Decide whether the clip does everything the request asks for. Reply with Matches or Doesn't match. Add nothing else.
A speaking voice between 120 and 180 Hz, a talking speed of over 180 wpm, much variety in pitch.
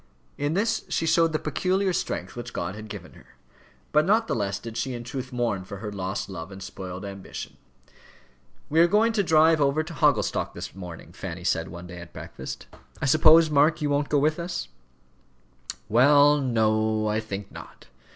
Matches